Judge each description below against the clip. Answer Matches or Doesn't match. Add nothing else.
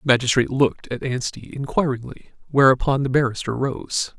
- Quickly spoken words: Doesn't match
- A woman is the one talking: Doesn't match